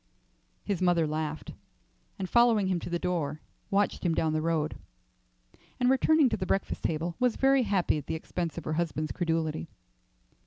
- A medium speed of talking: Yes, average, 170 wpm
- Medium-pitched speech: Yes, medium, 170 Hz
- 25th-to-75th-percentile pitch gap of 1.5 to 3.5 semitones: No, average, 4.2 semitones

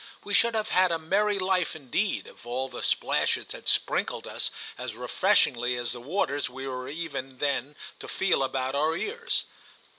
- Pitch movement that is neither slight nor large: No, wide, 6.7 semitones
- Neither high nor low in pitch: Yes, medium, 150 Hz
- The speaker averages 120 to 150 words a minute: No, average, 175 wpm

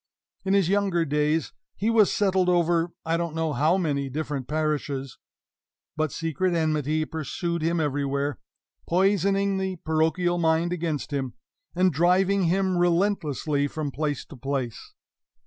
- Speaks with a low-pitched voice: No, medium, 160 Hz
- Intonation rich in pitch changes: No, average, 3.5 semitones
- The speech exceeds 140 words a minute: No, slow, 135 wpm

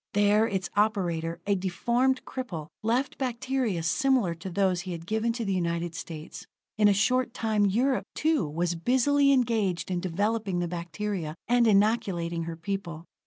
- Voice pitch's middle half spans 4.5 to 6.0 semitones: Yes, average, 5.3 semitones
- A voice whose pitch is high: Yes, high, 200 Hz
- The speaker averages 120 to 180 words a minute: Yes, average, 160 wpm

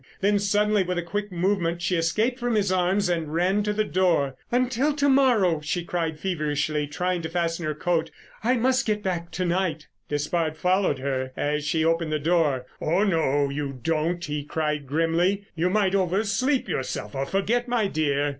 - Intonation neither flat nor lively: Yes, average, 4.7 semitones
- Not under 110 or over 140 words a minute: No, average, 185 wpm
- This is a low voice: No, medium, 175 Hz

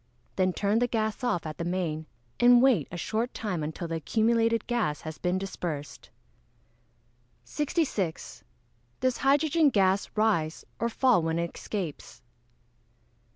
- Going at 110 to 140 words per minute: Yes, slow, 135 wpm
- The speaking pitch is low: No, high, 200 Hz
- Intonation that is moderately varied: No, wide, 6.3 semitones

